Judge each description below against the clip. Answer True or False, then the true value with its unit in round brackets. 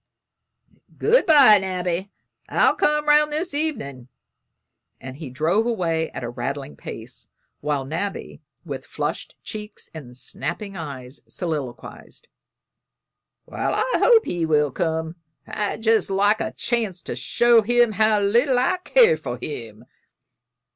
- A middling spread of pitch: False (7.8 semitones)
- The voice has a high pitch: True (195 Hz)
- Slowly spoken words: True (130 wpm)